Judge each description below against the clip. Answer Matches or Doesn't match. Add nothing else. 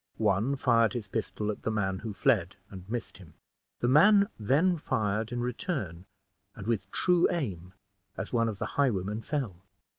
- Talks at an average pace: Matches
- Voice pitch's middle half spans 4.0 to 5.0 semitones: Matches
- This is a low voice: Matches